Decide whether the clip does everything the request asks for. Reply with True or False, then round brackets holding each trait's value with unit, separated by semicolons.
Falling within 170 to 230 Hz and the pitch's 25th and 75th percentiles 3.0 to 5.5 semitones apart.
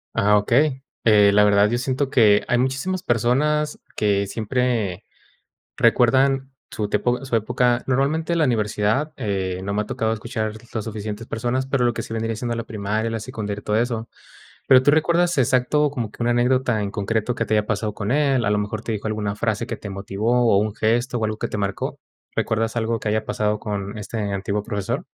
False (115 Hz; 3.3 semitones)